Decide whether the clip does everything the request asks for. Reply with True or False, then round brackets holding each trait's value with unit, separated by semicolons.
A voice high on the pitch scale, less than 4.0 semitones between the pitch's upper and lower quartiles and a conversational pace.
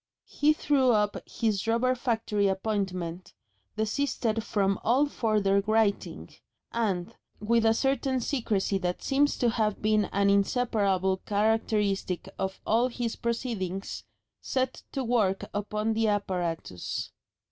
False (215 Hz; 3.2 semitones; 120 wpm)